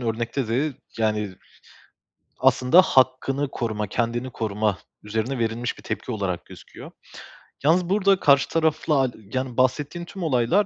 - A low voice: Yes, low, 130 Hz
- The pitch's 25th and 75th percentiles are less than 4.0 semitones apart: No, average, 4.7 semitones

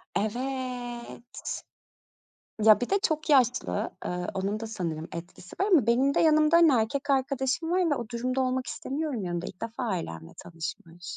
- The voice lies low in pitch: No, high, 245 Hz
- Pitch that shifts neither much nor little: No, wide, 5.8 semitones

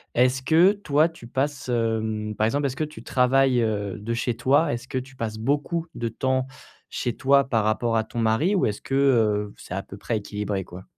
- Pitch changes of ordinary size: Yes, average, 3.8 semitones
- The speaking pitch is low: Yes, low, 120 Hz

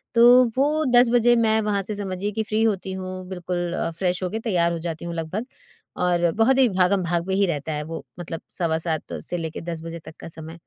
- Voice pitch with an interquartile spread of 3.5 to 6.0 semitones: Yes, average, 4.4 semitones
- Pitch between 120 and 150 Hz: No, medium, 185 Hz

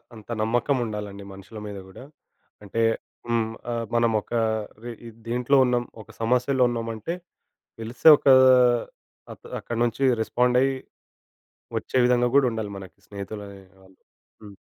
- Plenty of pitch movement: No, average, 2.8 semitones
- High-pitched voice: No, low, 115 Hz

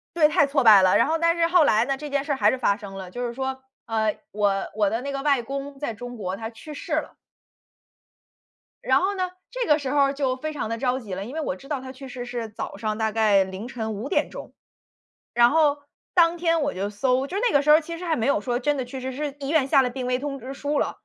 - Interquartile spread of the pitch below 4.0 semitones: No, average, 4.6 semitones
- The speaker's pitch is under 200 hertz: No, very high, 265 Hz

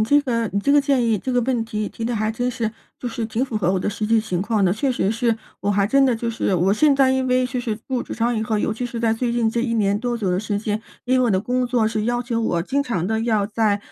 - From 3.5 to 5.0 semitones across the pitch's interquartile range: No, narrow, 2.6 semitones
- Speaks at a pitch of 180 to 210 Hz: No, high, 230 Hz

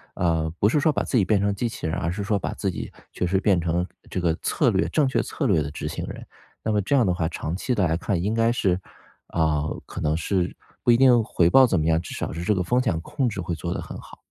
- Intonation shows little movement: No, average, 5.3 semitones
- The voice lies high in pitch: No, very low, 95 Hz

